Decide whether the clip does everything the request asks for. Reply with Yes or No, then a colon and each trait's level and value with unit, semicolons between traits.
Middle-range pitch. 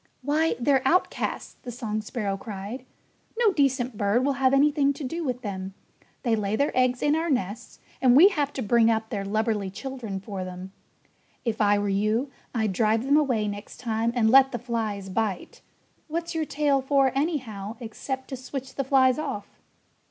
No: high, 245 Hz